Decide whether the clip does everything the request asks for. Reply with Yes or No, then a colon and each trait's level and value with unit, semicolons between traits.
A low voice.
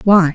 No: medium, 180 Hz